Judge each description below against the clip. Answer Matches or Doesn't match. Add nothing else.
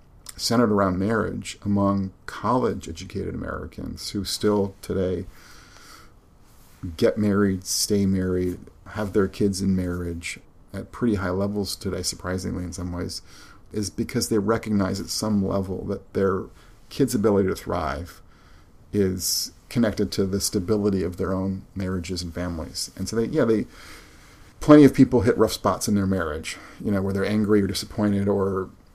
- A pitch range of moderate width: Doesn't match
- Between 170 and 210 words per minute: Doesn't match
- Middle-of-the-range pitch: Doesn't match